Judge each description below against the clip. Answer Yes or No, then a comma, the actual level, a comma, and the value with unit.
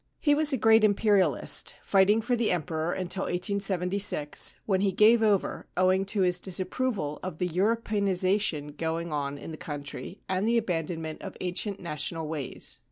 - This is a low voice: No, medium, 185 Hz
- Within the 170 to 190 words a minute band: No, average, 160 wpm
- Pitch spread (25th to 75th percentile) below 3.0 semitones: No, average, 4.1 semitones